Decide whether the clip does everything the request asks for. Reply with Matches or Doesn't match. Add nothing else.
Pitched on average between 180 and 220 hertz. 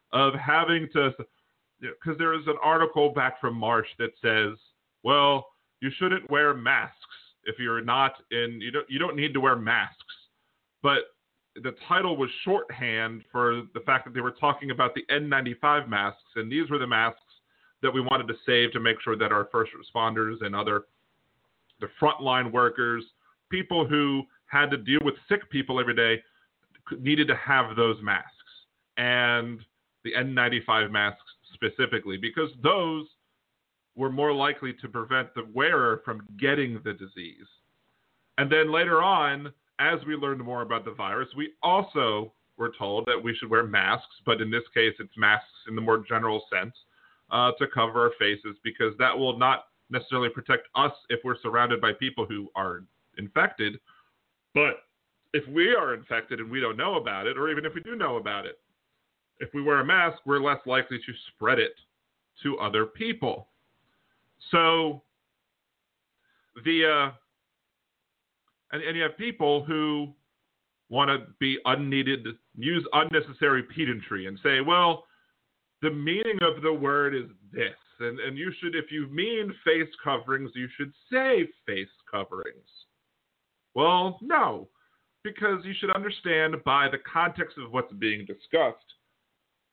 Doesn't match